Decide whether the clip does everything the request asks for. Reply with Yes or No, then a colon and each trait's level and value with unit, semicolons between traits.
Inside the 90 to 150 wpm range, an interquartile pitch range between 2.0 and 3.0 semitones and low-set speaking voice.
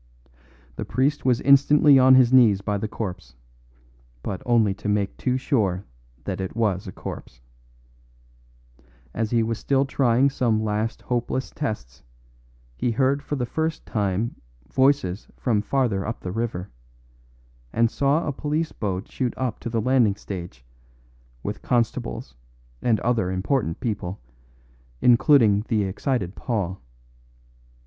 No: slow, 135 wpm; average, 4.8 semitones; low, 115 Hz